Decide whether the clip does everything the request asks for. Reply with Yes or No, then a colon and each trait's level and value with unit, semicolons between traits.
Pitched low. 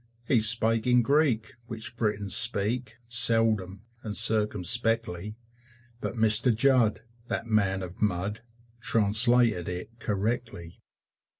Yes: low, 110 Hz